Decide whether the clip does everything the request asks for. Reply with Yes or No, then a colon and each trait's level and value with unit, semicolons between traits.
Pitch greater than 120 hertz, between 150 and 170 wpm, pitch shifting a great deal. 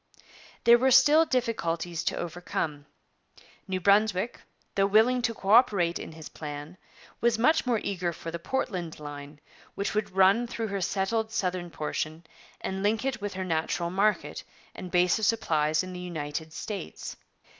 No: high, 190 Hz; average, 165 wpm; average, 4.9 semitones